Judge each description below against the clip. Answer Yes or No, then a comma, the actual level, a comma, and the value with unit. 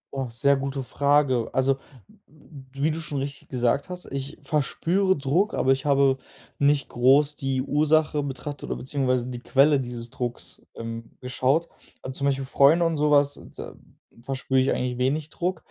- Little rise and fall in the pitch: Yes, narrow, 2.2 semitones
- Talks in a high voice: No, medium, 140 Hz